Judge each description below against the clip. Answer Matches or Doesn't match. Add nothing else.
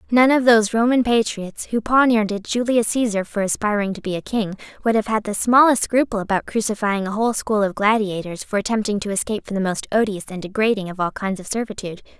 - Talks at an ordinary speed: Doesn't match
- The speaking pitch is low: Doesn't match